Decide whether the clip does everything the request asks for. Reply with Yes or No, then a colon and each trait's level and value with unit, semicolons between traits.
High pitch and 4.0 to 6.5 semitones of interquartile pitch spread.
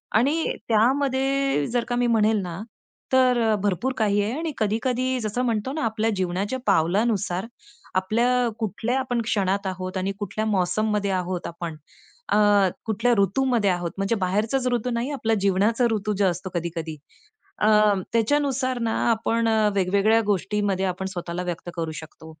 Yes: high, 215 Hz; average, 4.3 semitones